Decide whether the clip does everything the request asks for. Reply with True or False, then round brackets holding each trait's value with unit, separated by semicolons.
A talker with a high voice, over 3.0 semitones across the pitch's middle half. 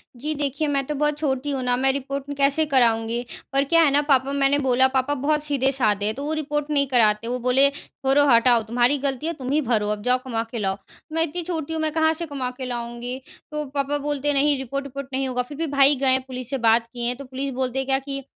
False (270 Hz; 2.5 semitones)